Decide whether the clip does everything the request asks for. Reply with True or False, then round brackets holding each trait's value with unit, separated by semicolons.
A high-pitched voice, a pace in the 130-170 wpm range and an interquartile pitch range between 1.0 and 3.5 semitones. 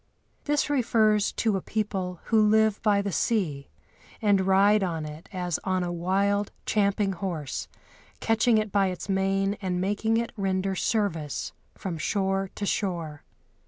True (195 Hz; 150 wpm; 2.5 semitones)